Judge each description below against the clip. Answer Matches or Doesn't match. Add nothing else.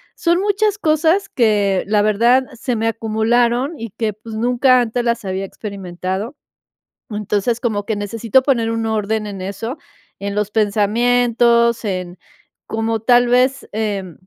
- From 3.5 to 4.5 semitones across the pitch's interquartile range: Doesn't match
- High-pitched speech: Matches